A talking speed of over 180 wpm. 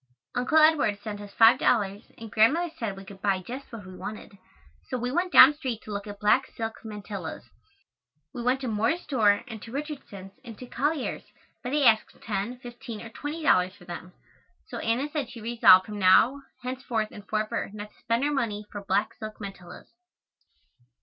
Yes: average, 190 wpm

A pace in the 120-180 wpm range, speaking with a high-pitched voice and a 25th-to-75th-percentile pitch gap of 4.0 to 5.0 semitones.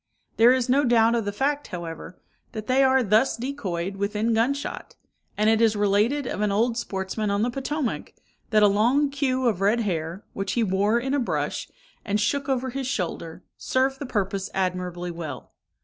No: average, 190 wpm; high, 220 Hz; average, 4.7 semitones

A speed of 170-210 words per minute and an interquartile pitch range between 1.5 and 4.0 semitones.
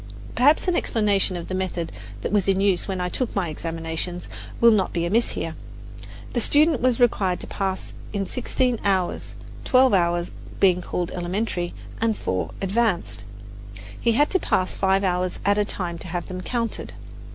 No: average, 175 wpm; average, 4.4 semitones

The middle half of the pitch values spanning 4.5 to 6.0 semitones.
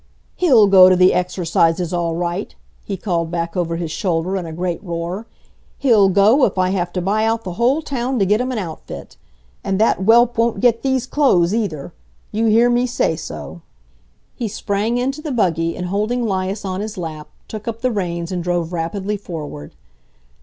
Yes: average, 4.8 semitones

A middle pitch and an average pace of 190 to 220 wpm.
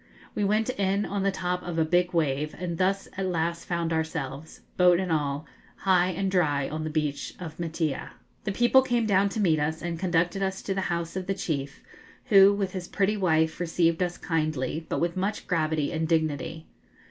Yes: medium, 175 Hz; average, 200 wpm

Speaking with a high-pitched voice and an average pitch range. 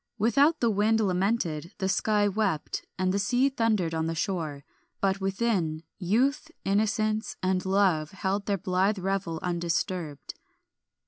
Yes: high, 195 Hz; average, 3.7 semitones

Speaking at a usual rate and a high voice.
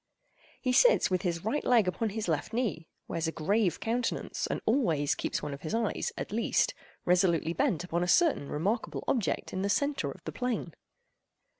Yes: average, 185 wpm; high, 195 Hz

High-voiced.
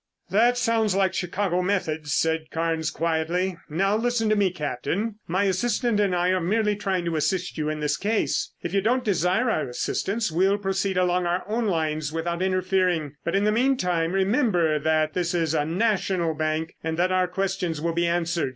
No: medium, 180 Hz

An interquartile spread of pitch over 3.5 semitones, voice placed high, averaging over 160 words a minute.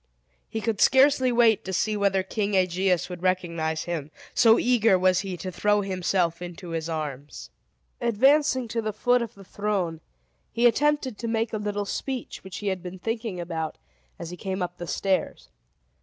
Yes: average, 4.2 semitones; high, 195 Hz; average, 180 wpm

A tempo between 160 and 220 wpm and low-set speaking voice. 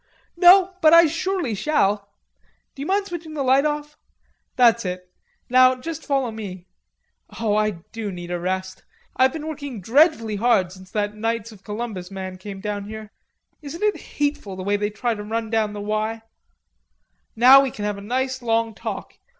No: average, 175 wpm; high, 225 Hz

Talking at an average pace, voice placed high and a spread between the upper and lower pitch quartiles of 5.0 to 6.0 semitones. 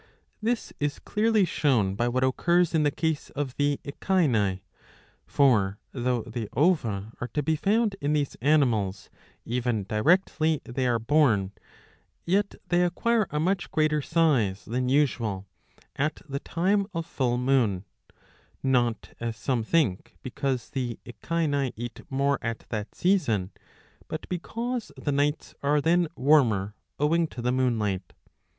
No: average, 145 wpm; medium, 140 Hz; wide, 5.6 semitones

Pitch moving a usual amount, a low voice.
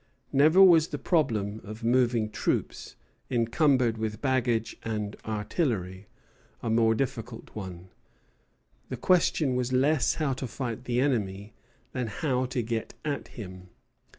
Yes: average, 3.8 semitones; low, 120 Hz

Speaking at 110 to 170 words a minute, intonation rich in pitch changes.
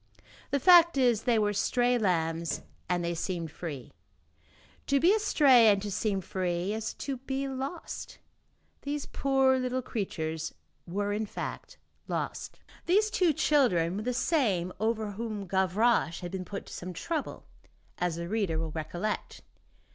Yes: average, 150 wpm; wide, 6.9 semitones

